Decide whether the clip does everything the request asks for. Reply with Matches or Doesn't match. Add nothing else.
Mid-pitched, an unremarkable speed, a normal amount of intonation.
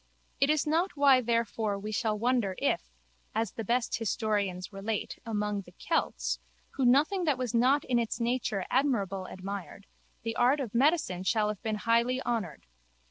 Doesn't match